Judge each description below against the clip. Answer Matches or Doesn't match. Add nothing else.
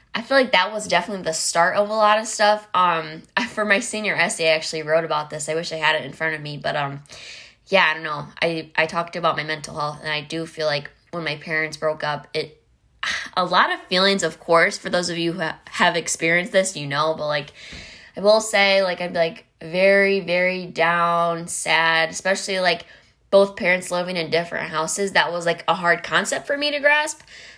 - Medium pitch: Matches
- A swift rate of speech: Matches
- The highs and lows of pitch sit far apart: Doesn't match